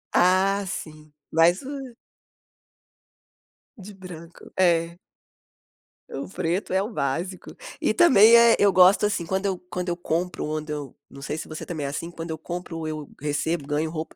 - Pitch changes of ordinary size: Yes, average, 3.5 semitones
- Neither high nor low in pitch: Yes, medium, 175 Hz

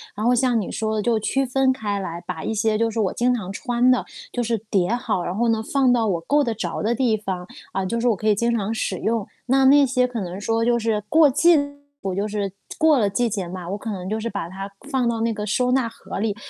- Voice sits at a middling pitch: No, high, 225 Hz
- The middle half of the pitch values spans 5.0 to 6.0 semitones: No, average, 3.4 semitones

